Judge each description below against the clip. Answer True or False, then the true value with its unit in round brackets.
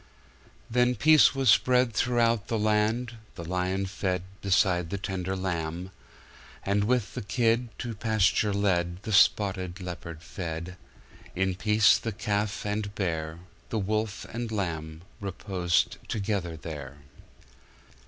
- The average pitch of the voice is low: True (100 Hz)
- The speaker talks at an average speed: False (115 wpm)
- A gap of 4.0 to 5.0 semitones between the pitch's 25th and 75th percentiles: False (3.5 semitones)